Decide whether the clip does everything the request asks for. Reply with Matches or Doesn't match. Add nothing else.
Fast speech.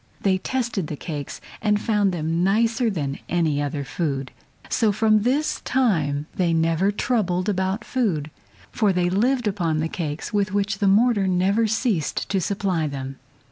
Doesn't match